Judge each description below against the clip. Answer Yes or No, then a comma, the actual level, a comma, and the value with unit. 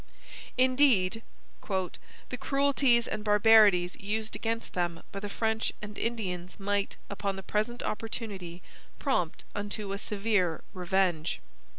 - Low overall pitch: No, high, 205 Hz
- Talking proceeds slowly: Yes, slow, 115 wpm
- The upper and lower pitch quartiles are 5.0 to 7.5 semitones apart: No, average, 3.3 semitones